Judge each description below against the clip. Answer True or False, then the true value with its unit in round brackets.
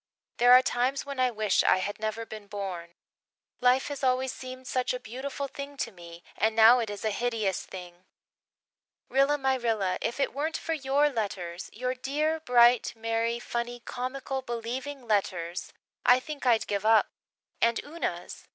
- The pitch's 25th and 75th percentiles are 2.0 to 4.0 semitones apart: True (3.6 semitones)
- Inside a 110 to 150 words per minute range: False (170 wpm)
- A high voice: True (240 Hz)